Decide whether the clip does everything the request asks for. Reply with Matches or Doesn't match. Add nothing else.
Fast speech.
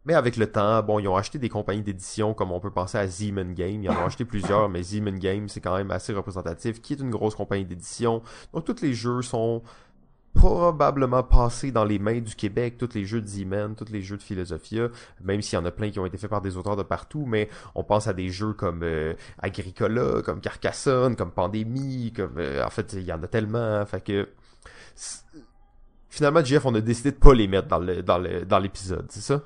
Matches